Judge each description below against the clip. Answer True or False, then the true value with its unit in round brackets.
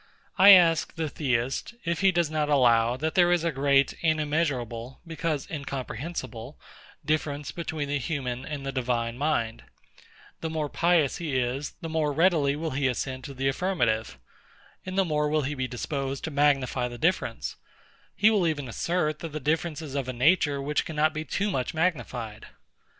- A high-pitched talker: False (145 Hz)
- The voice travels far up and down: False (3.8 semitones)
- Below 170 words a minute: False (175 wpm)